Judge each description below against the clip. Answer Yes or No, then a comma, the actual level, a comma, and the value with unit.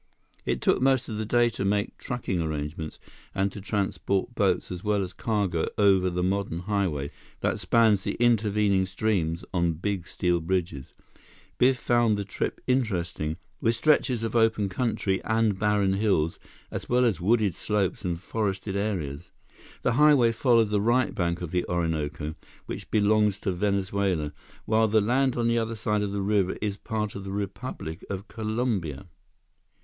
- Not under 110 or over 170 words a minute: Yes, average, 165 wpm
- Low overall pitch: Yes, low, 100 Hz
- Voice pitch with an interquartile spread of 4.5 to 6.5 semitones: No, average, 3.7 semitones